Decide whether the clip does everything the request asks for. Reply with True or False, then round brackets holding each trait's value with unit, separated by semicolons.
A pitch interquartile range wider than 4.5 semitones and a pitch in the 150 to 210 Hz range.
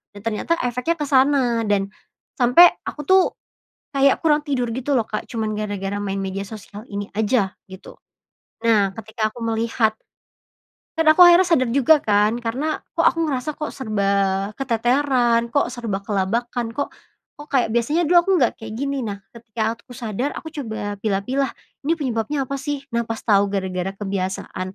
False (4.9 semitones; 235 Hz)